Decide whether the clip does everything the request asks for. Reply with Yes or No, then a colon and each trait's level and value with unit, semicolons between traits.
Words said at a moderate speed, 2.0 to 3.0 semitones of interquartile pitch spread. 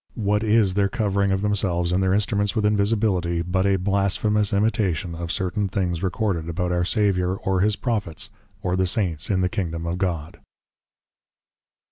Yes: average, 165 wpm; narrow, 2.6 semitones